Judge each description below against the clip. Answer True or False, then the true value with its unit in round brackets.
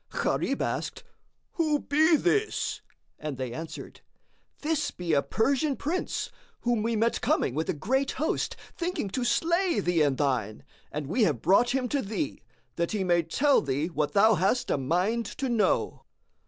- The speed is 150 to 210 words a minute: True (170 wpm)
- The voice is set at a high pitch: True (220 Hz)